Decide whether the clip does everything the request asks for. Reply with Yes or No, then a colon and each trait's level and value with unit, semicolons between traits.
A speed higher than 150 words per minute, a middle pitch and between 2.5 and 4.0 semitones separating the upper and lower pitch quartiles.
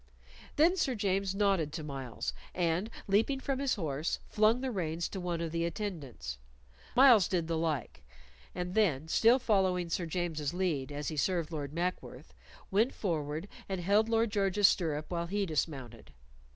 No: average, 165 wpm; medium, 175 Hz; average, 4.7 semitones